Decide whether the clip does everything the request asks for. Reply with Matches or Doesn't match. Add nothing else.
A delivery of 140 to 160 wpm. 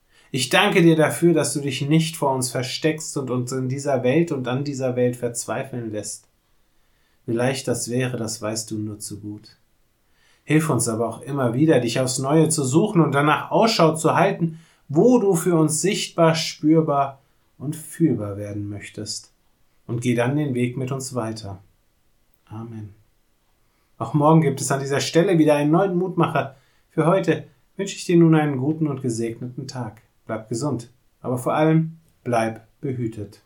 Doesn't match